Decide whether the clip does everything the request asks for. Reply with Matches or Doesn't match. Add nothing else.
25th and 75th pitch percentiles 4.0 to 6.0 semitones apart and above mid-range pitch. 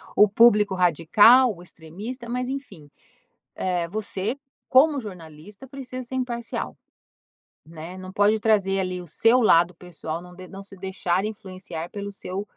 Matches